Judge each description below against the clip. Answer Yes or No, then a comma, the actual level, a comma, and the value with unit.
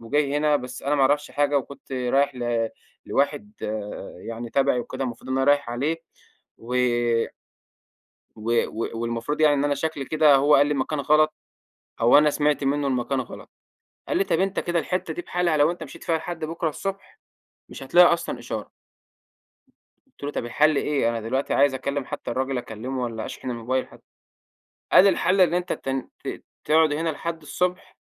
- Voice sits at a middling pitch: Yes, medium, 145 Hz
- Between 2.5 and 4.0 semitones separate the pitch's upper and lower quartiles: Yes, average, 3.6 semitones